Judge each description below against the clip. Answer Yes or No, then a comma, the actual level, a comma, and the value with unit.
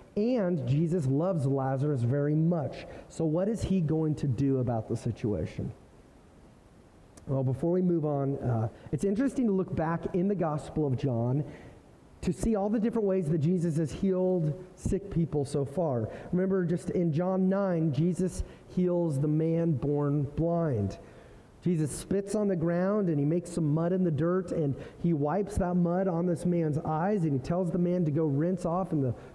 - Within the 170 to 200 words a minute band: Yes, average, 185 wpm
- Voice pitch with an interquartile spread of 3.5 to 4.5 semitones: Yes, average, 4.0 semitones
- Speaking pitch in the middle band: Yes, medium, 165 Hz